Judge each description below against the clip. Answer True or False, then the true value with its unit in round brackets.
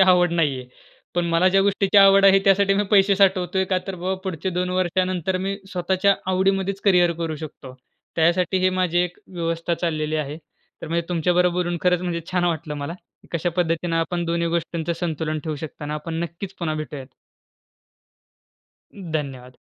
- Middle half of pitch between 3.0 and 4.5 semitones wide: False (2.4 semitones)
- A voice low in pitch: False (175 Hz)